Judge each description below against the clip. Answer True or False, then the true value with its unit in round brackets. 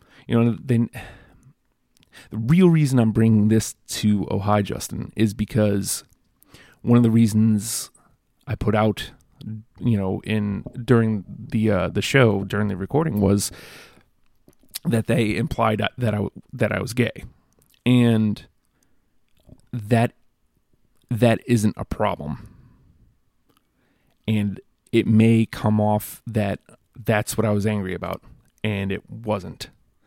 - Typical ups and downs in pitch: False (2.3 semitones)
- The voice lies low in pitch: True (110 Hz)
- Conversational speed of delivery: False (130 wpm)